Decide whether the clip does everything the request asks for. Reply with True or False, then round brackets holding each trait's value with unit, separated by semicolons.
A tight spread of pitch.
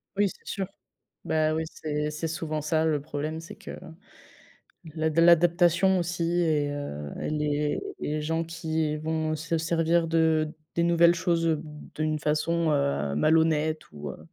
True (1.7 semitones)